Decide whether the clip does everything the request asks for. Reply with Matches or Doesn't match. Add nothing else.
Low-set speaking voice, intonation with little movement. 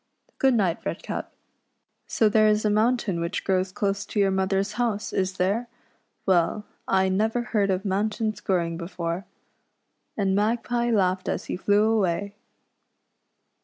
Doesn't match